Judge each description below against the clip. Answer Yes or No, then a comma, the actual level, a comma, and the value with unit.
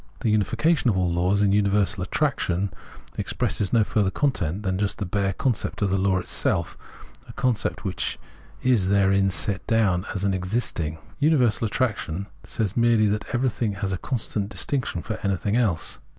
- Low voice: Yes, low, 100 Hz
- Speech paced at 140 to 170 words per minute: Yes, average, 165 wpm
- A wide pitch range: No, average, 3.4 semitones